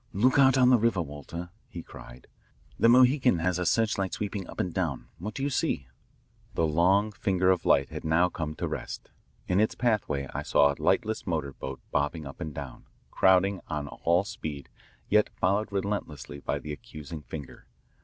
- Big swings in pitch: Yes, wide, 5.7 semitones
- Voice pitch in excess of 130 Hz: No, very low, 90 Hz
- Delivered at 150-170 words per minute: No, average, 185 wpm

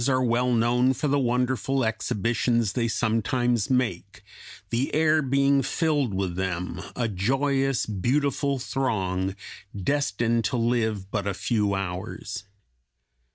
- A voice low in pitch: Yes, low, 120 Hz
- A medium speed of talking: No, slow, 125 wpm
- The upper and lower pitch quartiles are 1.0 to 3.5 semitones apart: No, average, 4.9 semitones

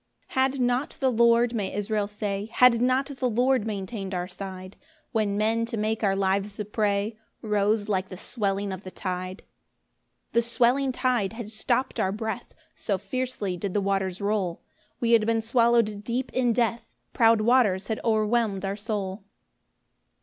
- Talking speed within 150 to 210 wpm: Yes, average, 170 wpm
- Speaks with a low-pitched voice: No, high, 215 Hz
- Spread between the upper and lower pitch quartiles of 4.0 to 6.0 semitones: No, average, 3.0 semitones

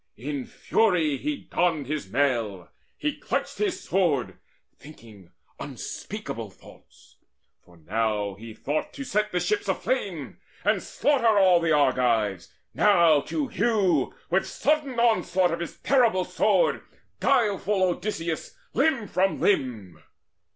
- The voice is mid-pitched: Yes, medium, 175 Hz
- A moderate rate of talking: No, slow, 125 wpm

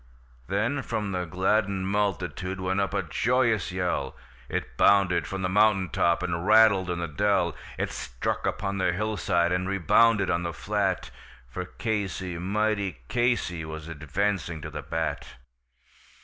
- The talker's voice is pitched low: Yes, very low, 95 Hz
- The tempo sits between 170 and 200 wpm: No, average, 150 wpm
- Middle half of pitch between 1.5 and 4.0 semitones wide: Yes, average, 3.0 semitones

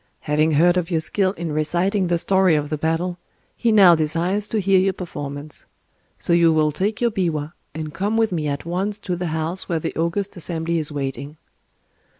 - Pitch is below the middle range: No, medium, 170 Hz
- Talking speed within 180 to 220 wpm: Yes, average, 195 wpm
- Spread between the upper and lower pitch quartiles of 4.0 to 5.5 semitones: No, average, 3.4 semitones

